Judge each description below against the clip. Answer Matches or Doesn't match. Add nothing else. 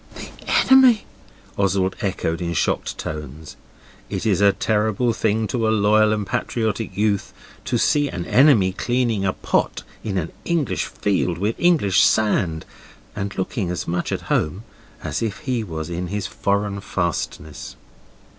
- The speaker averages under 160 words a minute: Matches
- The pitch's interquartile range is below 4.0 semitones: Matches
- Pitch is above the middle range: Doesn't match